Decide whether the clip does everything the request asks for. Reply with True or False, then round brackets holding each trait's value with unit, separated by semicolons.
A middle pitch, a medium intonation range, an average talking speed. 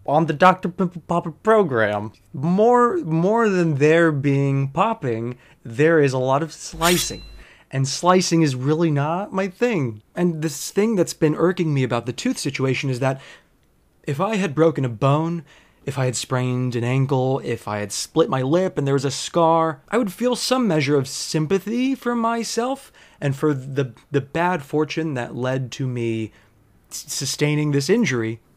True (150 Hz; 5.0 semitones; 180 wpm)